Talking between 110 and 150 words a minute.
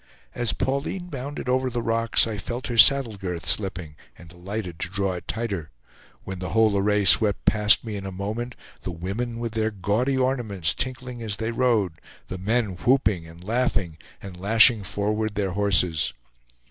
No: average, 170 wpm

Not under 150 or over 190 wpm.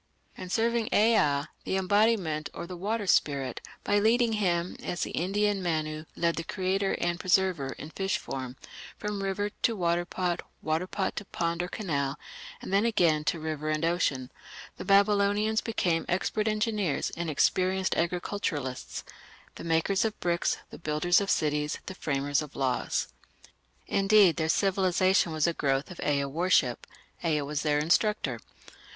Yes: average, 155 wpm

